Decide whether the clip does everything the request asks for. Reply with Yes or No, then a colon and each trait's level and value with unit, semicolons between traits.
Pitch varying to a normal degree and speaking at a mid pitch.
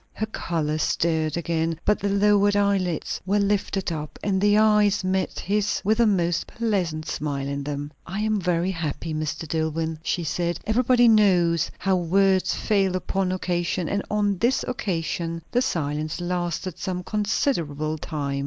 Yes: average, 4.1 semitones; medium, 180 Hz